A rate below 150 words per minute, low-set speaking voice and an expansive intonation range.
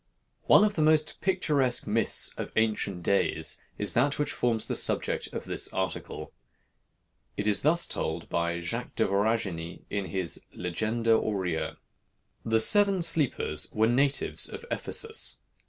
Yes: average, 140 wpm; low, 110 Hz; wide, 7.1 semitones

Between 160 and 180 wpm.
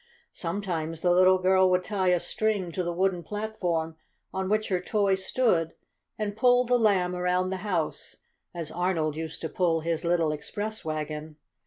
Yes: average, 170 wpm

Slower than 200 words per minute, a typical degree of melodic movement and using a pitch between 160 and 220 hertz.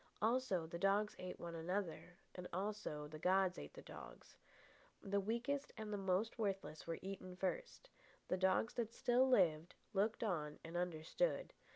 Yes: average, 160 wpm; average, 3.8 semitones; high, 190 Hz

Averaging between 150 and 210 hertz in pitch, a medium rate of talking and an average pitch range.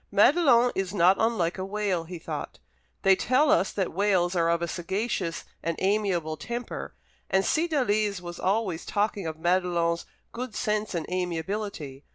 Yes: high, 190 Hz; average, 155 wpm; average, 3.7 semitones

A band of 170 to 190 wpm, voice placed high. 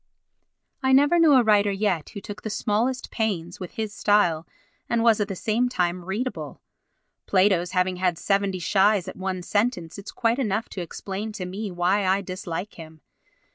Yes: average, 175 wpm; high, 200 Hz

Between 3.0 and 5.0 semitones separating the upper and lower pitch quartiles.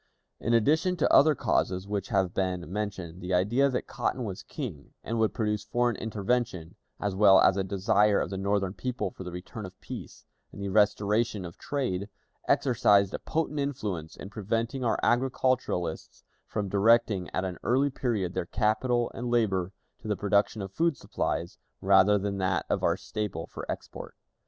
Yes: average, 4.0 semitones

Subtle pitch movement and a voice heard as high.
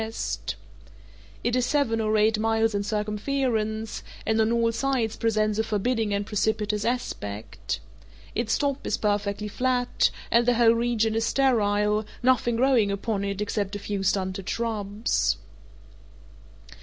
Yes: narrow, 2.2 semitones; high, 220 Hz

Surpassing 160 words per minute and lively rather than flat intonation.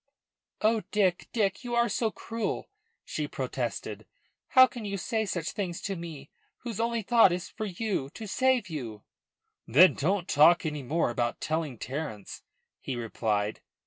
No: average, 155 wpm; wide, 7.4 semitones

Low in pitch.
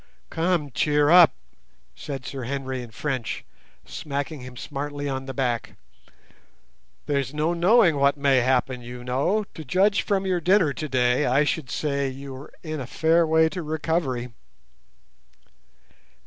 No: medium, 145 Hz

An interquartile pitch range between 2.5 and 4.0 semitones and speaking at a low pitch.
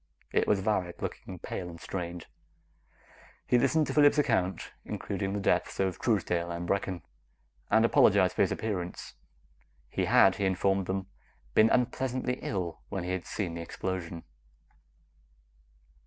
Yes: average, 3.7 semitones; very low, 95 Hz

